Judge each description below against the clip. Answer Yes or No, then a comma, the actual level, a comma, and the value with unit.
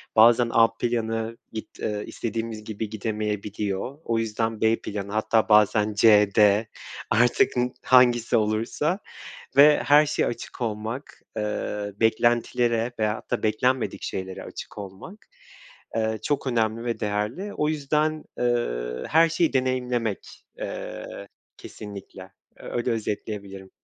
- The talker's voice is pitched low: Yes, low, 110 Hz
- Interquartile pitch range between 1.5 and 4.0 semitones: Yes, narrow, 2.4 semitones